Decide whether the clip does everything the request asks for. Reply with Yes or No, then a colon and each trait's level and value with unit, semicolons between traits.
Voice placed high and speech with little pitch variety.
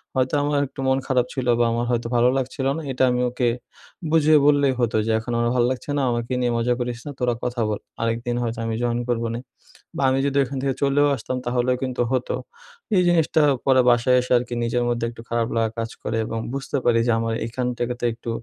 No: low, 120 Hz; narrow, 1.9 semitones